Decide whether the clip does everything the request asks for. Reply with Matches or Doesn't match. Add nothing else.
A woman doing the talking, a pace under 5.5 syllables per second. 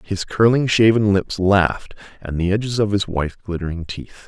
Doesn't match